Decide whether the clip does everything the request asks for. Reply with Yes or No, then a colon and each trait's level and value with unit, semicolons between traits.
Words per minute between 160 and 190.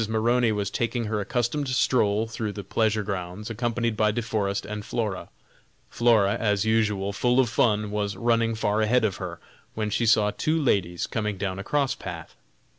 Yes: average, 180 wpm